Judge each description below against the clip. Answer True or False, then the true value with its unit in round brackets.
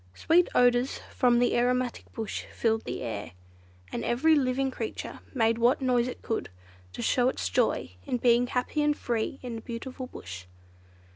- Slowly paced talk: False (165 wpm)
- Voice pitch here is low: False (245 Hz)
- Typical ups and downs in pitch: False (1.9 semitones)